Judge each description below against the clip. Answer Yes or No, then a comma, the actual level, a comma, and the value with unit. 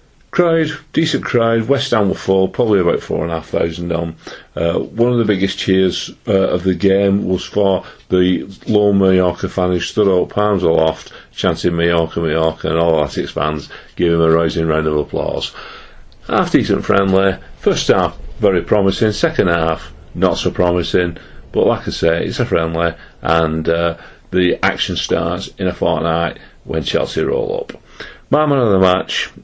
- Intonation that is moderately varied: Yes, average, 3.3 semitones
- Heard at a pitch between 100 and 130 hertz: No, very low, 90 Hz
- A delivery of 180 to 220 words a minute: No, average, 165 wpm